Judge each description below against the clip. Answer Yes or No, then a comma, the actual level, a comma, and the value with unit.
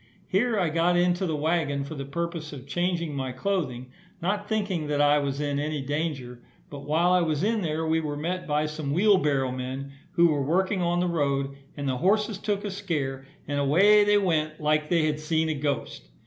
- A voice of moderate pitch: Yes, medium, 155 Hz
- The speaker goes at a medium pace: No, fast, 210 wpm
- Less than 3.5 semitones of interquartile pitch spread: No, average, 3.9 semitones